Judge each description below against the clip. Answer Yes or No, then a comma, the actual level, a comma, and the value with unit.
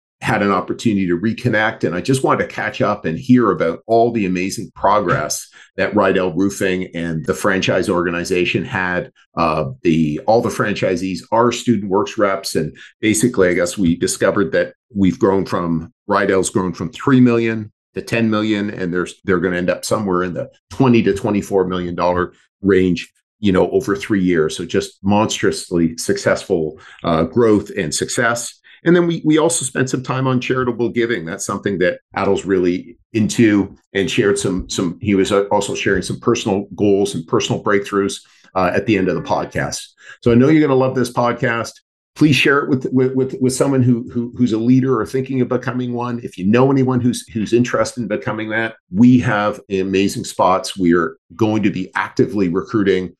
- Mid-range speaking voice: No, low, 105 Hz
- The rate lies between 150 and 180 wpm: No, average, 190 wpm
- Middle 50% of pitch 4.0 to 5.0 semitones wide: Yes, average, 4.7 semitones